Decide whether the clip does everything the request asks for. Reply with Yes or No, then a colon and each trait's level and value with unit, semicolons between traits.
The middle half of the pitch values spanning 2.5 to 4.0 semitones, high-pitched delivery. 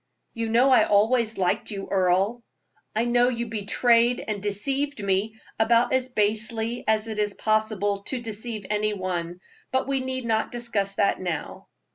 Yes: average, 2.8 semitones; high, 220 Hz